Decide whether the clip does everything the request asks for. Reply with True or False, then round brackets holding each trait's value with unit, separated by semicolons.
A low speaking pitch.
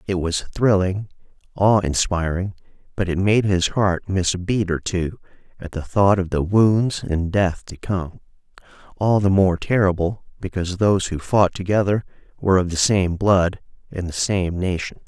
True (95 Hz)